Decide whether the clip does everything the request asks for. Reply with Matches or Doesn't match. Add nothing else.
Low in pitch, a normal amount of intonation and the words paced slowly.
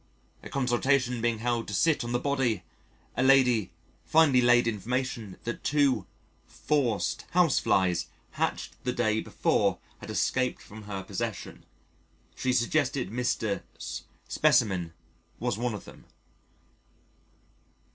Matches